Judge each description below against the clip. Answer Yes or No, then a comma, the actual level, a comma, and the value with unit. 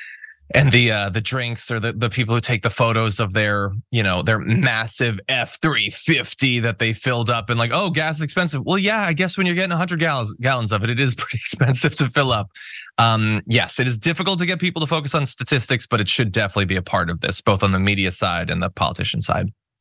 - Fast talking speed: Yes, fast, 240 wpm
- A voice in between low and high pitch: No, low, 120 Hz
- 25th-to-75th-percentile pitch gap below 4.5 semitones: No, wide, 5.5 semitones